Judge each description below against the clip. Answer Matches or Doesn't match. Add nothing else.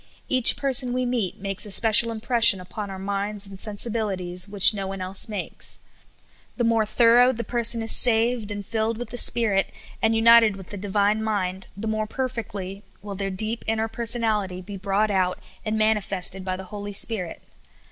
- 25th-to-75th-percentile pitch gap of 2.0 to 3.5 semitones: Matches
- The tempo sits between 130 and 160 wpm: Doesn't match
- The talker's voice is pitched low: Doesn't match